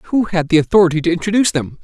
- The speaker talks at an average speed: No, fast, 230 wpm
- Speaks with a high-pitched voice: No, medium, 175 Hz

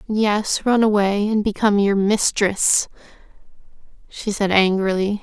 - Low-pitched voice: No, high, 205 Hz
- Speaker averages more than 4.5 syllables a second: No, 4.2 syllables/s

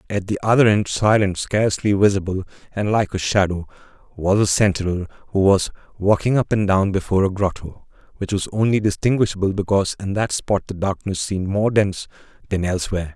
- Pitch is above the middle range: No, low, 100 Hz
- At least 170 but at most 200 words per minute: Yes, average, 175 wpm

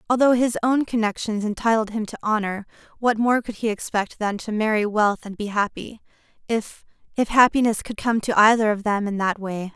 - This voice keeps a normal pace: Yes, average, 190 wpm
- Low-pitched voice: No, high, 215 Hz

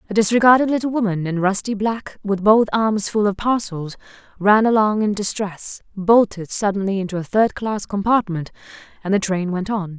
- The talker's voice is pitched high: Yes, high, 205 Hz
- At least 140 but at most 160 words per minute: No, average, 175 wpm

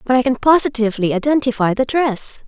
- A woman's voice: Yes, female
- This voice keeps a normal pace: Yes, average, 170 wpm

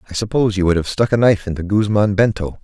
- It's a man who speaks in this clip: Yes, male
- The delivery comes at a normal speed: No, fast, 250 wpm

